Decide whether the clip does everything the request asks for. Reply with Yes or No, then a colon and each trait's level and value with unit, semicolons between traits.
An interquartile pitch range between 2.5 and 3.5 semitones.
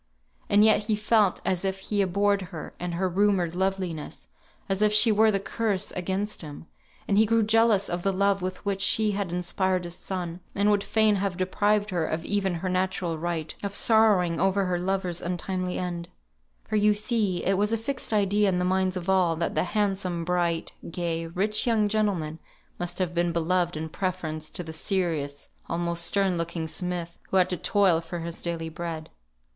Yes: average, 2.9 semitones